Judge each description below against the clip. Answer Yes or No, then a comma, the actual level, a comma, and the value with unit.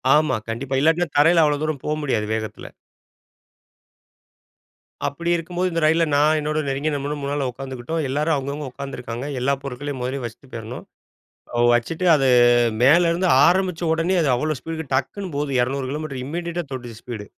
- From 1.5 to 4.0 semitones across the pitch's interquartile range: Yes, average, 3.6 semitones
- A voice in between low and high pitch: Yes, medium, 145 Hz